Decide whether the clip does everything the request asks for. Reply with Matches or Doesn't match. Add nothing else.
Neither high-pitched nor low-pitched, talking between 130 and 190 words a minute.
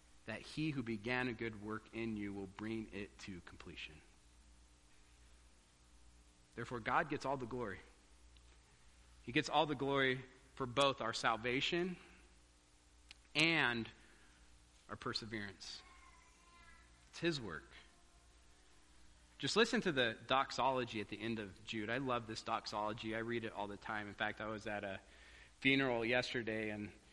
Doesn't match